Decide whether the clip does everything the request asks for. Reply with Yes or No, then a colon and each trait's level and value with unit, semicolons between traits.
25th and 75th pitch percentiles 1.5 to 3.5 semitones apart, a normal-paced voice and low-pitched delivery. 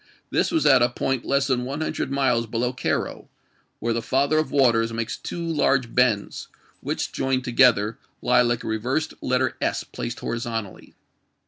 Yes: average, 2.7 semitones; average, 175 wpm; low, 125 Hz